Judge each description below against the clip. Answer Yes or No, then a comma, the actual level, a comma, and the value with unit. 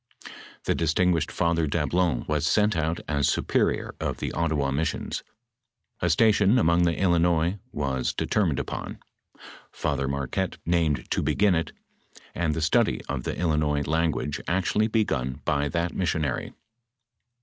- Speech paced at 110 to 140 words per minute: Yes, slow, 135 wpm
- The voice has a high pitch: No, very low, 80 Hz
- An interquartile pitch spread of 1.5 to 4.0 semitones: Yes, average, 3.1 semitones